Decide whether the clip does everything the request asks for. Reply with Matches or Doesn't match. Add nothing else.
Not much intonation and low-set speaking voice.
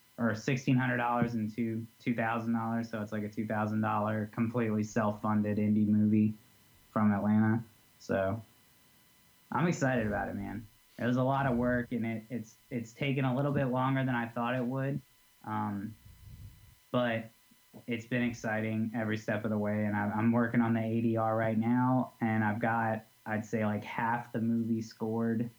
Matches